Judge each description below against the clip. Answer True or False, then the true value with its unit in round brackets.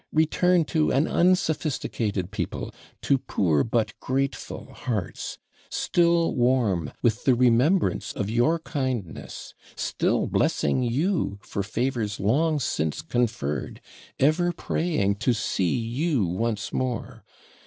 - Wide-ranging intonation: True (6.7 semitones)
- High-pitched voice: False (125 Hz)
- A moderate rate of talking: False (110 wpm)